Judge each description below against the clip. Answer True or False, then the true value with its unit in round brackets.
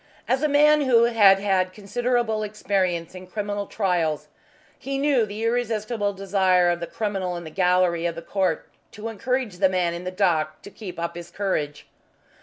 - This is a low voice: False (195 Hz)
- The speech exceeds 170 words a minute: True (180 wpm)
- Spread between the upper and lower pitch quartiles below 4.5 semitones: True (3.8 semitones)